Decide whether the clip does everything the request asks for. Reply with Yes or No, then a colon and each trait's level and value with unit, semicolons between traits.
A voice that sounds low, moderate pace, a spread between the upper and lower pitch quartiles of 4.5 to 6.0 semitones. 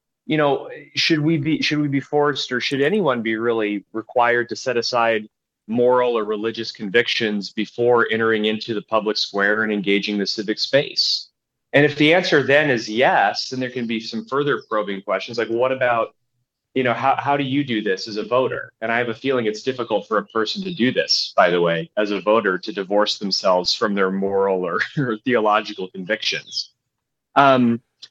No: low, 115 Hz; average, 195 wpm; average, 3.7 semitones